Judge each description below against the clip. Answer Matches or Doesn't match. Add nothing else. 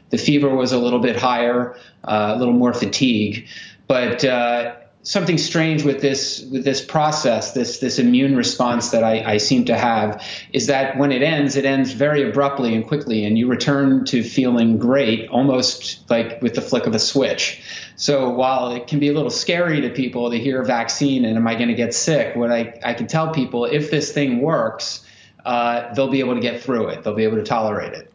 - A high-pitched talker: Doesn't match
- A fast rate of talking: Matches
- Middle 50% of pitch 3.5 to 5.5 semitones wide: Doesn't match